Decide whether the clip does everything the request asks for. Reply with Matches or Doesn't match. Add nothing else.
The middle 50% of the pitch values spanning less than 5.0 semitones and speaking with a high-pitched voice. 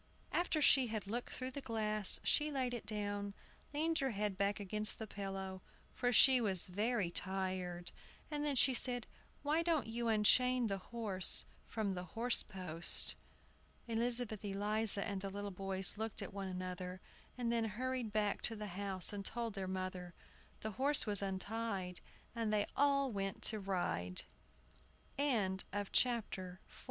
Matches